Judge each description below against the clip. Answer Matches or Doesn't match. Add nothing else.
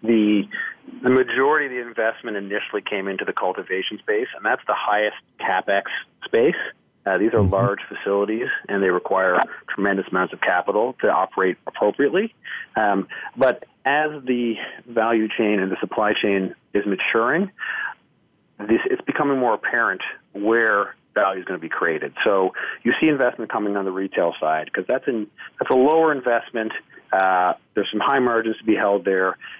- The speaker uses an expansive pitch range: Doesn't match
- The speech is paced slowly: Doesn't match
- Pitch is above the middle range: Doesn't match